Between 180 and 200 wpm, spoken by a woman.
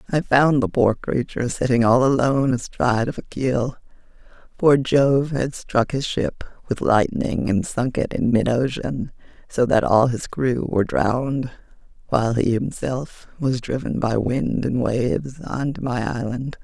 No: average, 165 wpm; female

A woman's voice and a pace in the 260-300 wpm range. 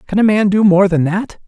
Yes: female; fast, 285 wpm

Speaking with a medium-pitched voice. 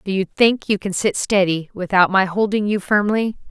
No: high, 195 Hz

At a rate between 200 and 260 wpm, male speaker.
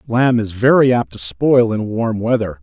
Yes: fast, 205 wpm; male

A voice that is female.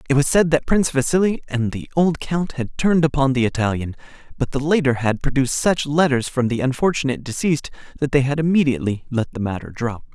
No: male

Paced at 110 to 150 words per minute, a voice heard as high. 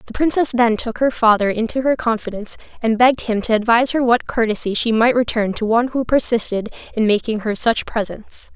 No: fast, 205 wpm; high, 230 Hz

